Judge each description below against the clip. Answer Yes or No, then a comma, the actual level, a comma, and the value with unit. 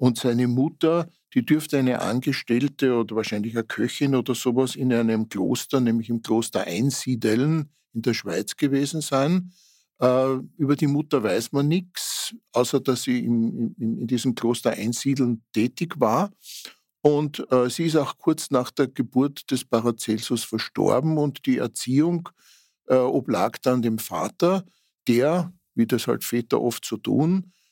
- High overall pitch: No, low, 130 Hz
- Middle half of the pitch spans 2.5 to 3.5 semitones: No, average, 4.4 semitones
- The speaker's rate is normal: Yes, average, 145 wpm